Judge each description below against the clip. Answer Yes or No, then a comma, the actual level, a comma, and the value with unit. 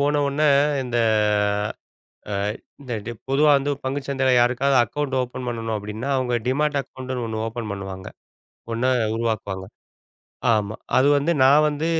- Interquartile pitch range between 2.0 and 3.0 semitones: No, average, 3.7 semitones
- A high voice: No, low, 130 Hz